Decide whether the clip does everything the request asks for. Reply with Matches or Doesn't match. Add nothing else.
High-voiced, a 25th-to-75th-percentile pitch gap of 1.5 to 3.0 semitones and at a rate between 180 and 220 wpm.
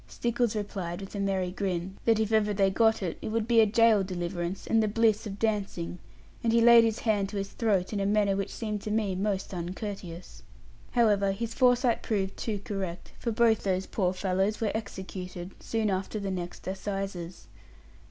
Matches